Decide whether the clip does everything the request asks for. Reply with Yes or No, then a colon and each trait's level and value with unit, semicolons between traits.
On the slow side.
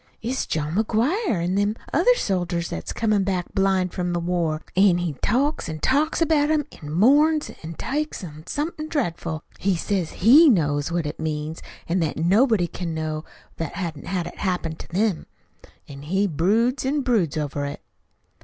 No: average, 175 wpm